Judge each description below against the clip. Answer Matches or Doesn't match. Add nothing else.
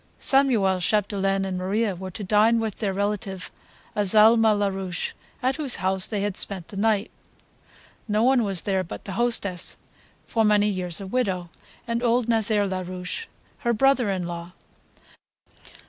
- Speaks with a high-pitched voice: Matches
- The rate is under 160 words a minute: Matches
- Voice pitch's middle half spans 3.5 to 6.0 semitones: Doesn't match